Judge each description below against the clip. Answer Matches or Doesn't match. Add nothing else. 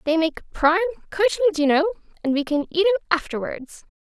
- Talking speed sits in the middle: Matches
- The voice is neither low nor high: Doesn't match